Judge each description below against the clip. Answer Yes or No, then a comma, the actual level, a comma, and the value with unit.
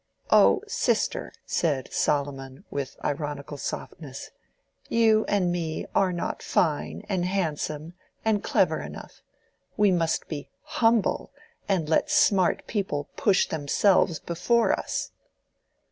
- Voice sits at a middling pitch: Yes, medium, 175 Hz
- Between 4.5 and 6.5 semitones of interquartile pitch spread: Yes, wide, 5.6 semitones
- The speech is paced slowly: Yes, slow, 115 wpm